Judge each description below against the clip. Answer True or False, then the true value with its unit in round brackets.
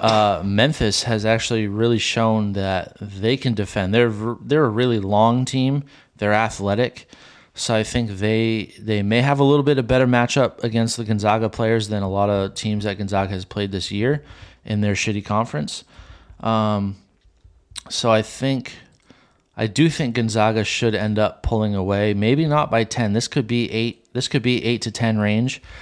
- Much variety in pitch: False (2.5 semitones)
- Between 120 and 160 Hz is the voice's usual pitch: False (110 Hz)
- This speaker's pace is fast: False (180 wpm)